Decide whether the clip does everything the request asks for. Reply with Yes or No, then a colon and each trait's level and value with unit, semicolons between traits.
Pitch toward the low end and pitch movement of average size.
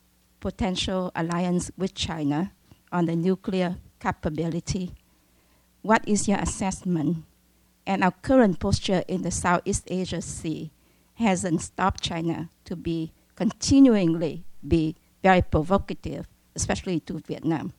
No: medium, 170 Hz; average, 3.0 semitones